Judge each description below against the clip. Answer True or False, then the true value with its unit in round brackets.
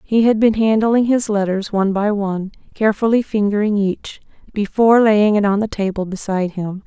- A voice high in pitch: True (210 Hz)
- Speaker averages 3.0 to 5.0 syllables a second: False (5.5 syllables/s)